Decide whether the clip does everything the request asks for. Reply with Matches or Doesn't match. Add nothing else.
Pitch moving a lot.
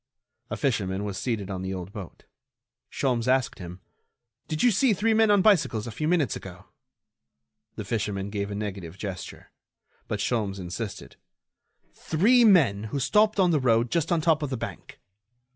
Matches